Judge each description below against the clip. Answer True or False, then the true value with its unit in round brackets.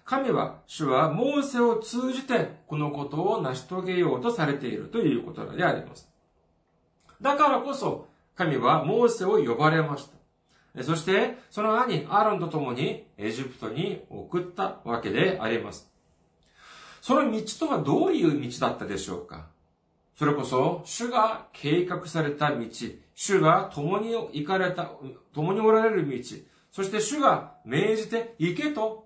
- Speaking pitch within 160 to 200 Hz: True (190 Hz)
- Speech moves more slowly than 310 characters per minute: True (285 characters per minute)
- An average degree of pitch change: False (7.6 semitones)